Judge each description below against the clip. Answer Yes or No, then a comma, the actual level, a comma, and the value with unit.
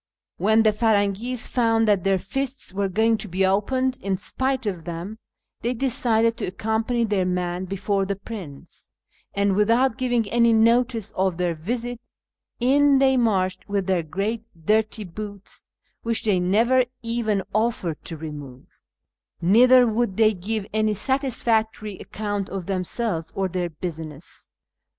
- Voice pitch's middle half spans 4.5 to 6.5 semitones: No, average, 3.7 semitones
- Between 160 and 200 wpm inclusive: No, average, 145 wpm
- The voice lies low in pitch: No, high, 210 Hz